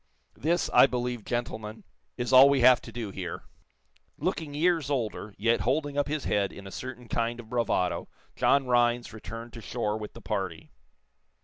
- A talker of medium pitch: No, low, 120 Hz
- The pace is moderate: Yes, average, 175 wpm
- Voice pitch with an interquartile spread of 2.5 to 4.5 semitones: Yes, average, 3.4 semitones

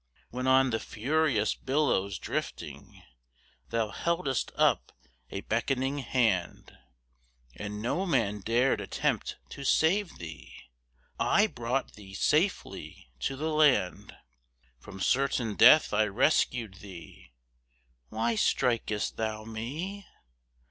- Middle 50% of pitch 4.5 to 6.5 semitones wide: Yes, average, 5.0 semitones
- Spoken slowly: Yes, slow, 105 wpm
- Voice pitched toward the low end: Yes, low, 120 Hz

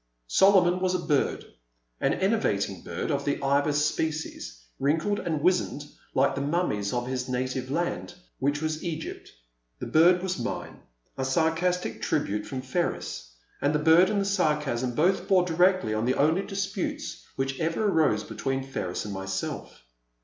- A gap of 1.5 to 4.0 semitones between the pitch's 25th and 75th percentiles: No, wide, 5.4 semitones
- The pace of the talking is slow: No, average, 155 wpm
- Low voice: No, medium, 150 Hz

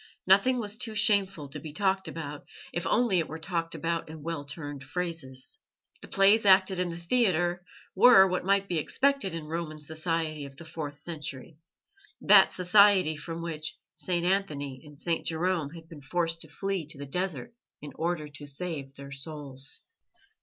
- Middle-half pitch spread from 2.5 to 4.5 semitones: Yes, average, 4.0 semitones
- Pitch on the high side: No, medium, 165 Hz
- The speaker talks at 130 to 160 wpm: No, average, 175 wpm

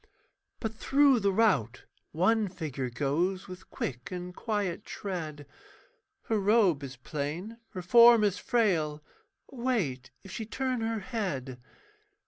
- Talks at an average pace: No, slow, 125 wpm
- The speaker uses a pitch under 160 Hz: No, high, 190 Hz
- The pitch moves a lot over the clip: Yes, wide, 7.0 semitones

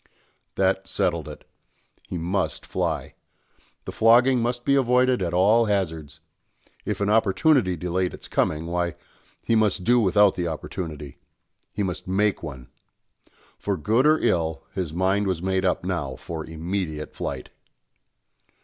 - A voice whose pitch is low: Yes, very low, 95 Hz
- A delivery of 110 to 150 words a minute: Yes, average, 140 wpm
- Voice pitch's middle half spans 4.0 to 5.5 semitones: Yes, average, 4.3 semitones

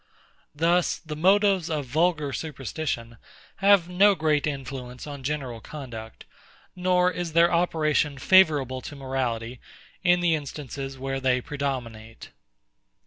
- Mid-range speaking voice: Yes, medium, 145 Hz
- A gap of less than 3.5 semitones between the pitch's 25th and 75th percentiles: No, average, 4.5 semitones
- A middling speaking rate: No, slow, 120 wpm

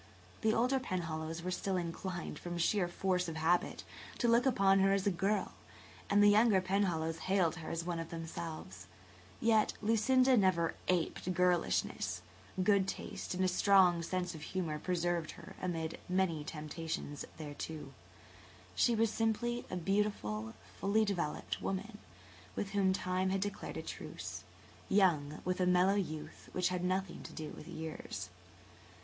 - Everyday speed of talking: Yes, average, 155 wpm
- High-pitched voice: No, medium, 180 Hz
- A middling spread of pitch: Yes, average, 3.4 semitones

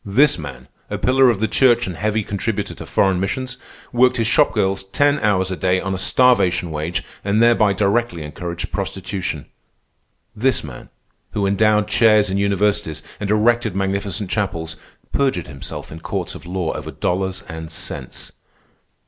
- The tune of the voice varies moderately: Yes, average, 3.7 semitones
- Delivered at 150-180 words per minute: Yes, average, 160 wpm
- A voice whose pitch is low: Yes, low, 100 Hz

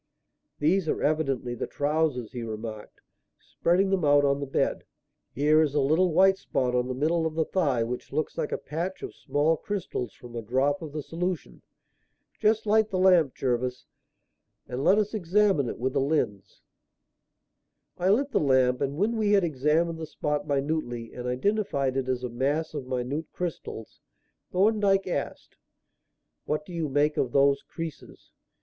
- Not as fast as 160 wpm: No, average, 170 wpm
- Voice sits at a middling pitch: Yes, medium, 150 Hz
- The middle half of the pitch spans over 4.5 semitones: Yes, wide, 5.5 semitones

